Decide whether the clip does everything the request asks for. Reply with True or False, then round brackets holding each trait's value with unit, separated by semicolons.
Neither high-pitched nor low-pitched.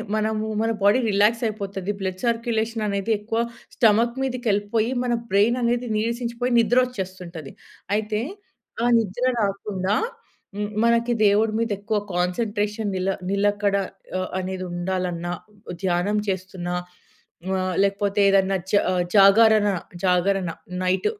False (205 Hz)